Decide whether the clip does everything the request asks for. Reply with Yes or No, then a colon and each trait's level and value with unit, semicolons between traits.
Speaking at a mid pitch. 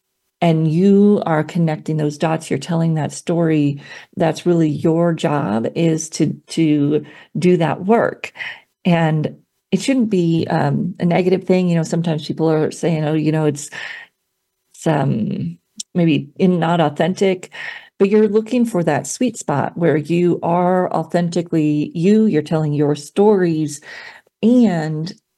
Yes: medium, 170 Hz